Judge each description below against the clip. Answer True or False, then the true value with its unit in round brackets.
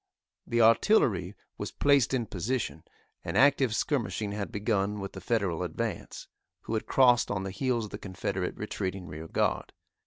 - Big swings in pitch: False (3.8 semitones)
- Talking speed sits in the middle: True (160 wpm)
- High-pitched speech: False (105 Hz)